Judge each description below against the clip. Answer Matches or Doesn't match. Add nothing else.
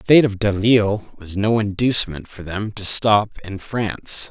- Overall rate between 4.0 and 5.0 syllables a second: Matches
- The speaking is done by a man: Matches